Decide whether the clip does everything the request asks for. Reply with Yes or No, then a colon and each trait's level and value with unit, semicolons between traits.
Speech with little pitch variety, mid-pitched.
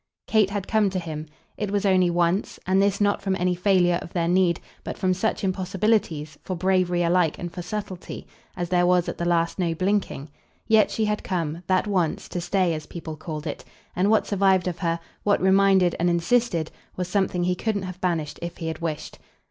Yes: narrow, 2.3 semitones; medium, 180 Hz